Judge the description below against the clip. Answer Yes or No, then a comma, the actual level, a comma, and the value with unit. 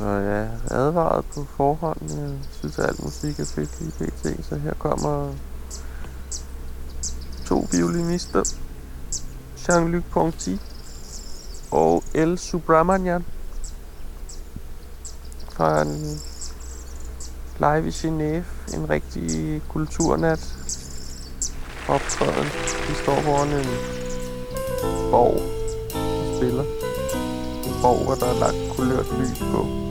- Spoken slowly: Yes, slow, 100 wpm